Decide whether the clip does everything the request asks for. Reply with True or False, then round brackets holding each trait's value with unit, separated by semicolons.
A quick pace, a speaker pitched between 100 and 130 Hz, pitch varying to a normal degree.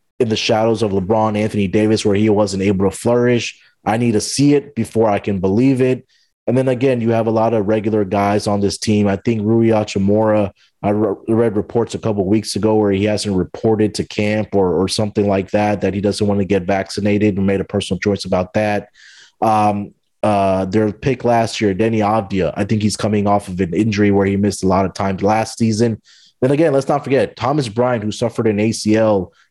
False (225 wpm; 105 Hz; 1.9 semitones)